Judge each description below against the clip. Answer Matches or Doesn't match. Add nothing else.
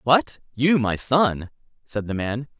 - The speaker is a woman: Doesn't match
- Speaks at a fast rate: Doesn't match